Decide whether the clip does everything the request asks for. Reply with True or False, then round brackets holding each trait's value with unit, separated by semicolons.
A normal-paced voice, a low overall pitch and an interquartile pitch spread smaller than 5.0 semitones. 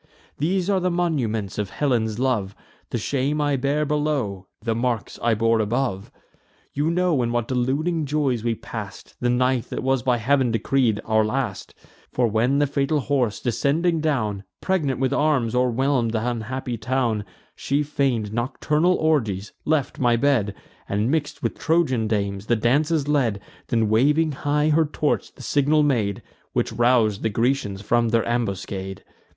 True (160 wpm; 125 Hz; 4.6 semitones)